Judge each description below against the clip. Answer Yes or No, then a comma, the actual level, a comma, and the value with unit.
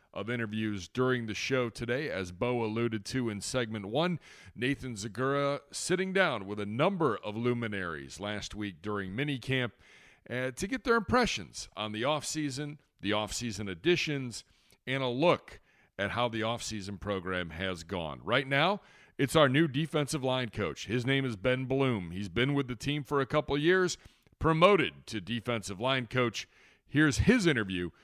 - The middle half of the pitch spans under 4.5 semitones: No, average, 5.2 semitones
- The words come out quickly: No, average, 165 wpm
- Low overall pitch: Yes, low, 125 Hz